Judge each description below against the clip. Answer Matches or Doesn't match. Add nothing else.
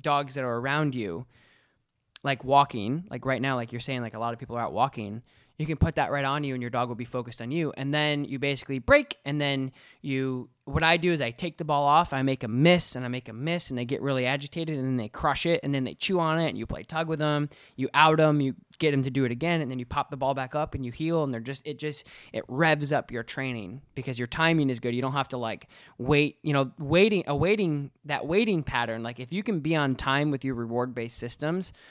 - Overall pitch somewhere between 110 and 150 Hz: Matches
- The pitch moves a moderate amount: Matches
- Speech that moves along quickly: Matches